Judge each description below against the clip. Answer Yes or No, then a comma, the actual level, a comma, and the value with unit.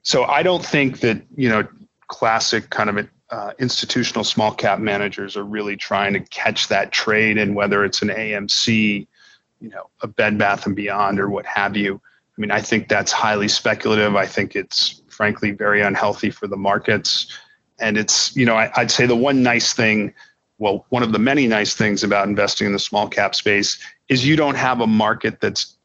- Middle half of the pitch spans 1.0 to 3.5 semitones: Yes, narrow, 2.4 semitones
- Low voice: Yes, low, 105 Hz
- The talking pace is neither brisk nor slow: Yes, average, 195 wpm